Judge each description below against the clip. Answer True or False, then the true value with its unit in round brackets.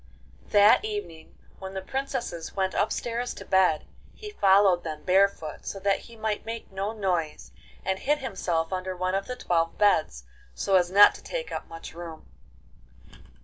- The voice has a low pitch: False (190 Hz)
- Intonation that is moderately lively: True (3.9 semitones)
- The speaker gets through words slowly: False (170 wpm)